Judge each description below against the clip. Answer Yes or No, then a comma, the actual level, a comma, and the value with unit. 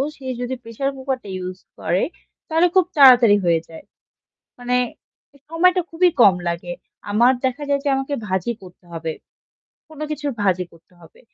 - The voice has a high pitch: Yes, high, 245 Hz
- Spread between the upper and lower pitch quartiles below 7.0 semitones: No, wide, 7.5 semitones